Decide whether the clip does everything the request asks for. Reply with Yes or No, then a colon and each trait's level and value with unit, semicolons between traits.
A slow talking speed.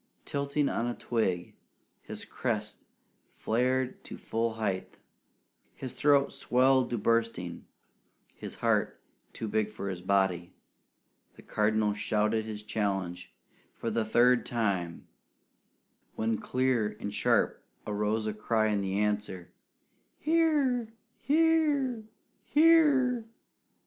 Yes: slow, 110 wpm